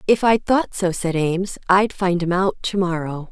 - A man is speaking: No, female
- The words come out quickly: Yes, fast, 215 wpm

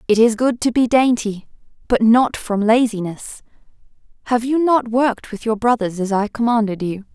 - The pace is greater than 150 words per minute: Yes, average, 175 wpm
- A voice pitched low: No, high, 225 Hz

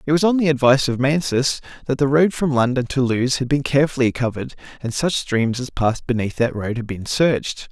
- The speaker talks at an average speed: No, fast, 225 wpm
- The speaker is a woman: No, male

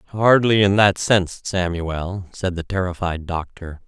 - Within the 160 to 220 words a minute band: No, average, 140 wpm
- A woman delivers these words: No, male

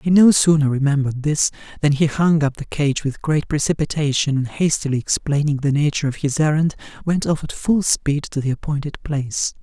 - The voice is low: No, medium, 150 Hz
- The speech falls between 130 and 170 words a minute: No, average, 195 wpm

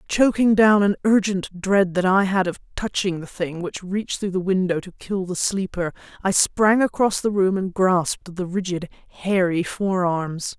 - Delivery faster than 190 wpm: No, average, 180 wpm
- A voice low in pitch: No, high, 190 Hz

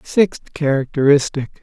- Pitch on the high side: No, medium, 150 Hz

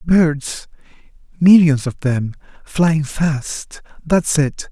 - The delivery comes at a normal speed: No, slow, 65 wpm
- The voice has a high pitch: No, medium, 150 Hz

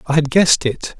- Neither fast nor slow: No, fast, 240 wpm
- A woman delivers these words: No, male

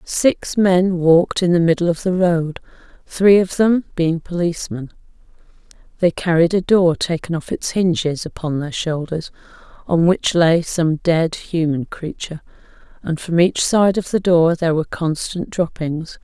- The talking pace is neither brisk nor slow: Yes, average, 160 wpm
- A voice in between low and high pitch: Yes, medium, 170 Hz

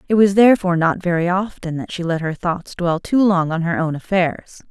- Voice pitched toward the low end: No, medium, 180 Hz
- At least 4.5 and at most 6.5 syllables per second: Yes, 5.4 syllables/s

